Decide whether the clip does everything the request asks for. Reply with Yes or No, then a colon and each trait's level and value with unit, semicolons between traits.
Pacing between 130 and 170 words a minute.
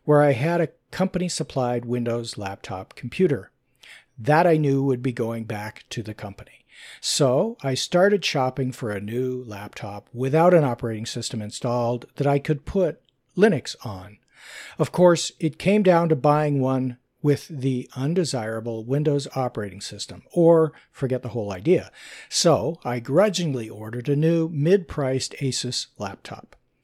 Yes: average, 150 wpm